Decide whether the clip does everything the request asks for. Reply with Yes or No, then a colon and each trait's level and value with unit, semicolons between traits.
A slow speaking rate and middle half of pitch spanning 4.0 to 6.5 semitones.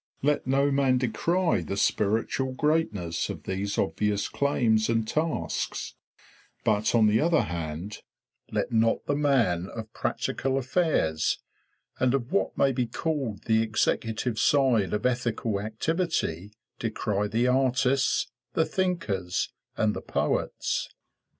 Yes: slow, 125 wpm; average, 4.7 semitones